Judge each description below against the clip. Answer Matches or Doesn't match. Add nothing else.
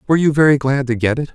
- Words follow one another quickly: Matches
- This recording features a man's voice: Matches